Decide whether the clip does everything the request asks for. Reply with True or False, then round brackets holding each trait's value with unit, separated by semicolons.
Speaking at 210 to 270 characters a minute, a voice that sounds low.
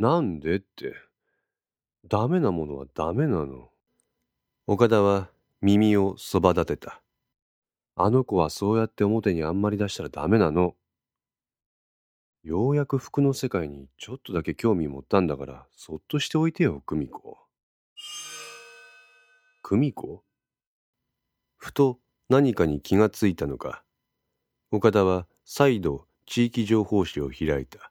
True (245 characters per minute; 105 Hz)